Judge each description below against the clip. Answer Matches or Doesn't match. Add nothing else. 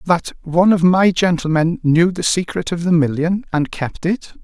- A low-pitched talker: Doesn't match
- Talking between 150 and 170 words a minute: Doesn't match